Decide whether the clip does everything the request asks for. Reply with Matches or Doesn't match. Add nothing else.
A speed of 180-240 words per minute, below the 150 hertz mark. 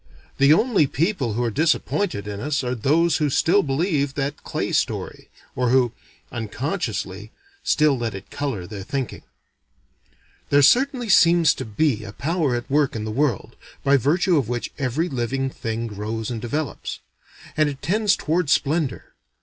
Doesn't match